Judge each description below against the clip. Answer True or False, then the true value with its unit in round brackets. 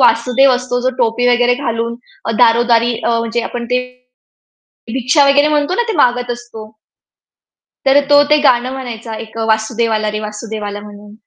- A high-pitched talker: True (240 Hz)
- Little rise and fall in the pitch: True (2.0 semitones)